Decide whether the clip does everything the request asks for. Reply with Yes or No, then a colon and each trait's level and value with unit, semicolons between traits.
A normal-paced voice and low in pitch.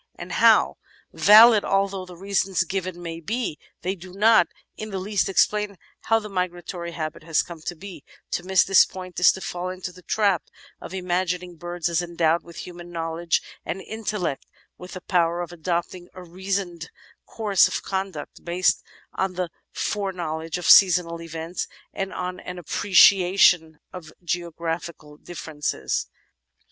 No: average, 155 wpm; medium, 180 Hz